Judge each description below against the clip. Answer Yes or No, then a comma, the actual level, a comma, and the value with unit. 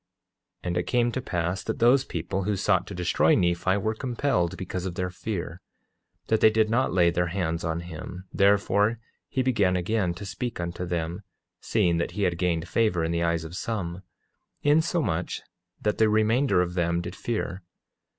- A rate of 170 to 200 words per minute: Yes, average, 185 wpm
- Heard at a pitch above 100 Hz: No, very low, 90 Hz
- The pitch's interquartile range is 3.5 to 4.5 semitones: Yes, average, 4.1 semitones